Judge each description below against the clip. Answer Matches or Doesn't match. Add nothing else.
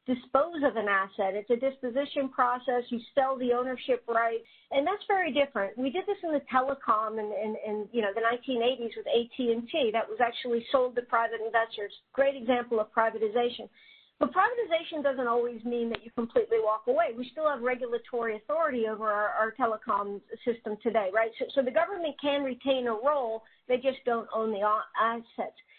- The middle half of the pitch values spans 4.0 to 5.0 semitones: Doesn't match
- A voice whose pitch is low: Doesn't match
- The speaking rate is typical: Matches